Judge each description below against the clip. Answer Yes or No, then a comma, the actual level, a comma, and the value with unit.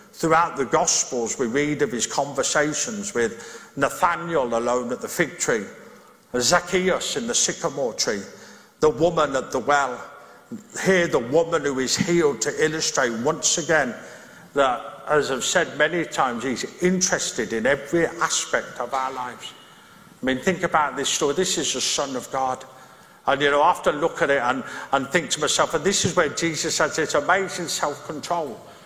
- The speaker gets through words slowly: No, average, 175 wpm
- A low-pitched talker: No, medium, 155 Hz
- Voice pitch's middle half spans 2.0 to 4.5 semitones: No, average, 4.9 semitones